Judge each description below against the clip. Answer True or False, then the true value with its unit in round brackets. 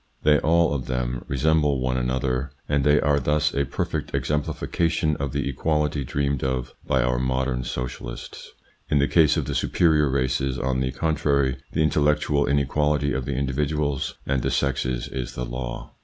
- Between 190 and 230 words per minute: False (170 wpm)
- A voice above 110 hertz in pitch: False (70 Hz)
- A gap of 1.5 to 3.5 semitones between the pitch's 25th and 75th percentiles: True (2.5 semitones)